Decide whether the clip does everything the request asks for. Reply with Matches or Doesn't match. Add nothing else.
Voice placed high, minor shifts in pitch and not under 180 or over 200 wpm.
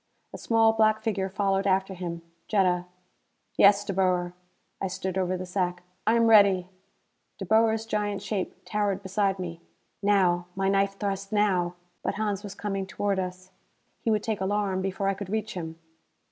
Doesn't match